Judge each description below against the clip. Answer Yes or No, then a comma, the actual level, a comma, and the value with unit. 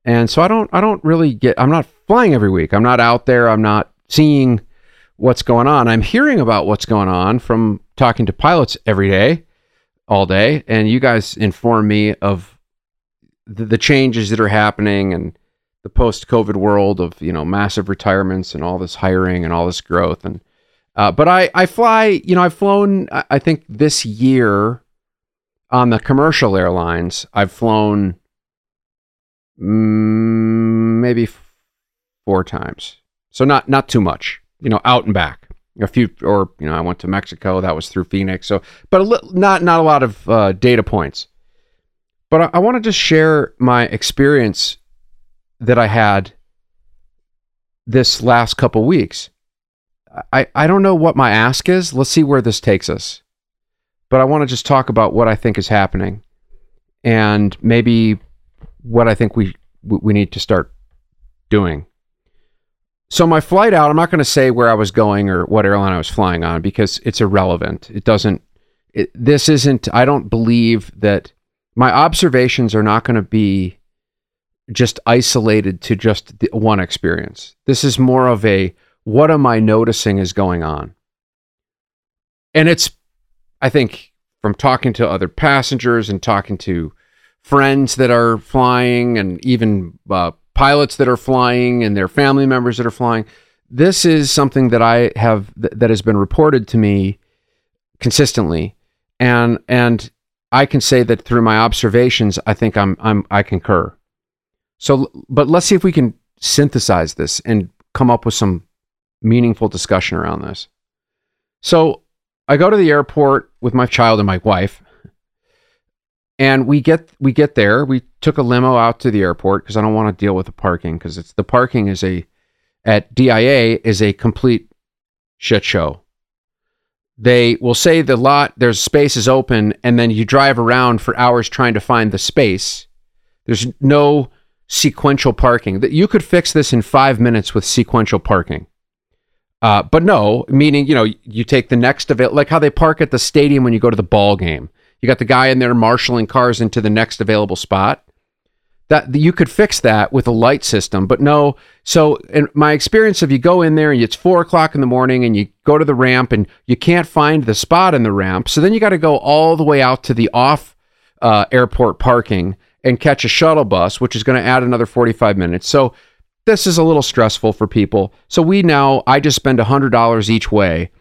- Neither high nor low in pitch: No, low, 115 Hz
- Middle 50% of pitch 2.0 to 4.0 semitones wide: No, average, 4.9 semitones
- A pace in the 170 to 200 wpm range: Yes, average, 185 wpm